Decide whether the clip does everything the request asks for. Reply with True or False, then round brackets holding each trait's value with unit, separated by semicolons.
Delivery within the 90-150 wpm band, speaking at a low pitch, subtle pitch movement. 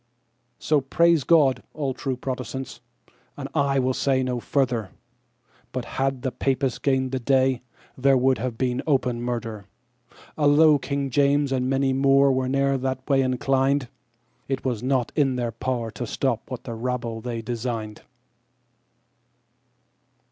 True (135 wpm; 130 Hz; 2.0 semitones)